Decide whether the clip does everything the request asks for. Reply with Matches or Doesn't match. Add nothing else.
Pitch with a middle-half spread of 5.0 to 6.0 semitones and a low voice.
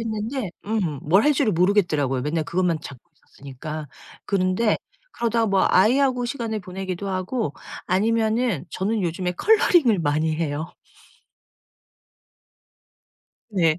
Doesn't match